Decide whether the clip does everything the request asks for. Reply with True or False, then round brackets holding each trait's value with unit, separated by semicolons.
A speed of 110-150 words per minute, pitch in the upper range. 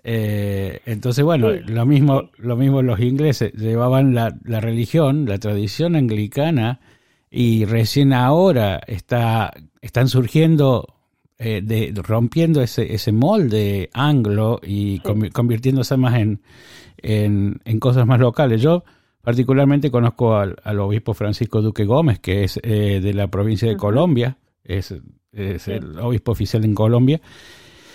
False (135 wpm; 115 Hz)